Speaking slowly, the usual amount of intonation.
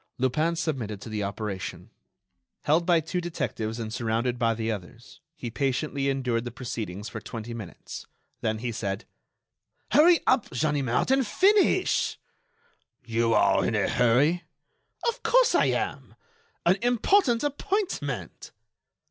No: slow, 130 wpm; wide, 7.4 semitones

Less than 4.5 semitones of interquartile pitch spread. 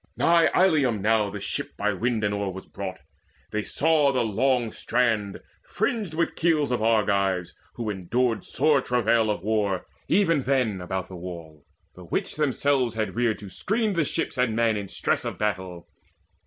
No: average, 5.2 semitones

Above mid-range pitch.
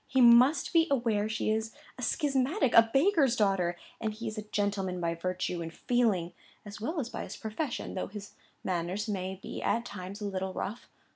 Yes: high, 215 Hz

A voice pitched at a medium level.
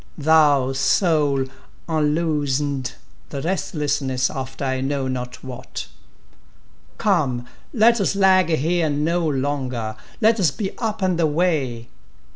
Yes: medium, 145 Hz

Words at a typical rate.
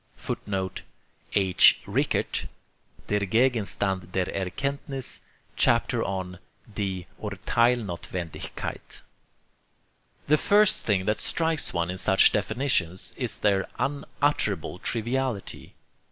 No: slow, 90 wpm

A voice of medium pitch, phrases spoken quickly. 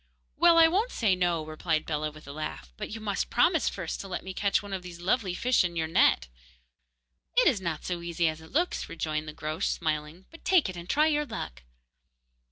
Yes: medium, 175 Hz; fast, 220 wpm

